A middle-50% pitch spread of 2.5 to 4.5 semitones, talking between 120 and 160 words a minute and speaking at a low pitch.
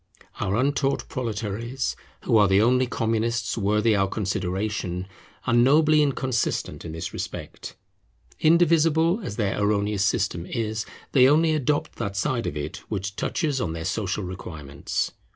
No: average, 5.3 semitones; average, 140 wpm; low, 110 Hz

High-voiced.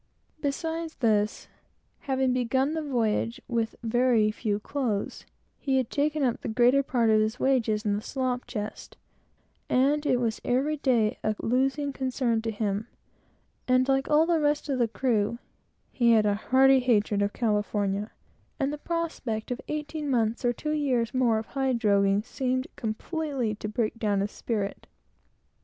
Yes: high, 245 Hz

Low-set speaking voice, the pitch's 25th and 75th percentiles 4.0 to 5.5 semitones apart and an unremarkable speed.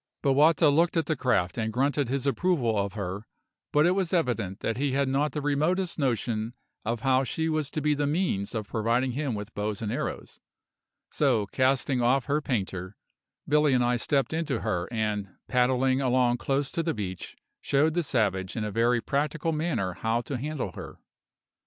Yes: low, 130 Hz; average, 5.1 semitones; average, 185 wpm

